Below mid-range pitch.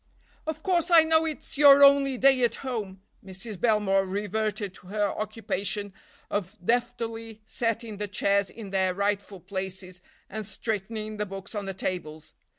No: high, 210 Hz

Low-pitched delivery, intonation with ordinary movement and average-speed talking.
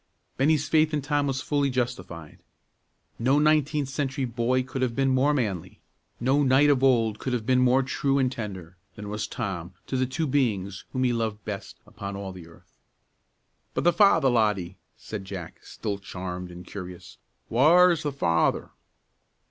No: low, 125 Hz; wide, 5.7 semitones; average, 170 wpm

